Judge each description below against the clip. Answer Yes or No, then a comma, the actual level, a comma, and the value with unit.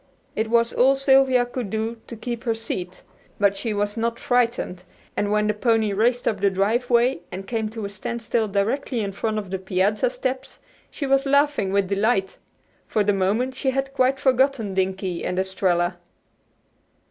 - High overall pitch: Yes, high, 220 Hz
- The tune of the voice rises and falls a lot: No, average, 4.0 semitones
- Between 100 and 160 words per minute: No, average, 175 wpm